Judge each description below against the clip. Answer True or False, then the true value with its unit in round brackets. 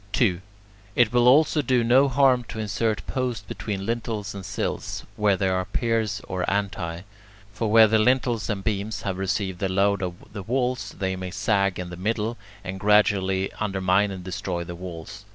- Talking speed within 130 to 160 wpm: False (180 wpm)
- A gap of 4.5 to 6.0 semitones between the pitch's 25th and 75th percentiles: False (3.3 semitones)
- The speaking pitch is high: False (100 Hz)